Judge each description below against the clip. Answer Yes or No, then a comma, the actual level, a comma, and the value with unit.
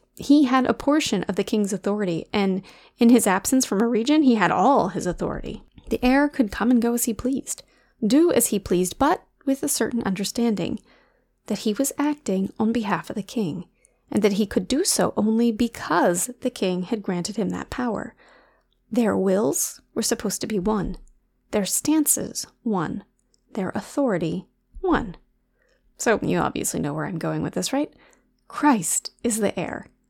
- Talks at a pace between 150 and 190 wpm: Yes, average, 175 wpm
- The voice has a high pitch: Yes, high, 225 Hz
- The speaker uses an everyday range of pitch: Yes, average, 4.5 semitones